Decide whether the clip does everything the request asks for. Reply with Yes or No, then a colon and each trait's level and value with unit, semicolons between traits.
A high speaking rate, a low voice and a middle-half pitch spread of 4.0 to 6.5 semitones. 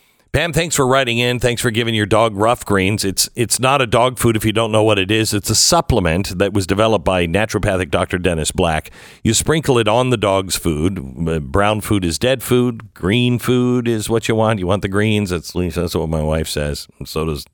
Yes: fast, 230 wpm; low, 105 Hz; average, 4.6 semitones